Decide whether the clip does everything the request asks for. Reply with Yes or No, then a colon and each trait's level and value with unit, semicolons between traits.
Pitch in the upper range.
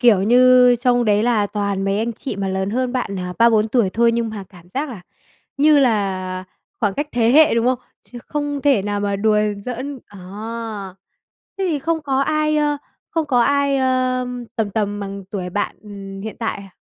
Yes: high, 235 Hz